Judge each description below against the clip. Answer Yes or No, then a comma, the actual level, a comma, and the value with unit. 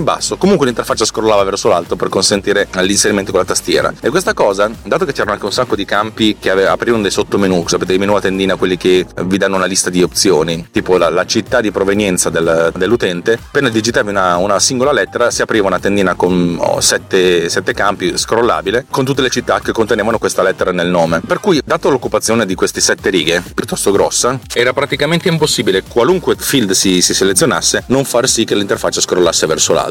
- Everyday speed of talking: No, fast, 205 wpm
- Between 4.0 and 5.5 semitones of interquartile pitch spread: No, average, 3.5 semitones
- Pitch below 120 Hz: Yes, very low, 95 Hz